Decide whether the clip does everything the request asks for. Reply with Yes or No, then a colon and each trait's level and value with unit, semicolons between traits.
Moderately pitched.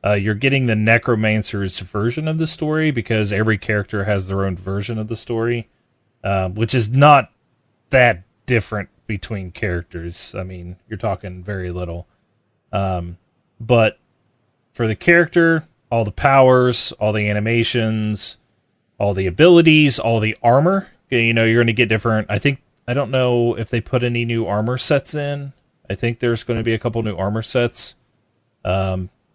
No: low, 115 Hz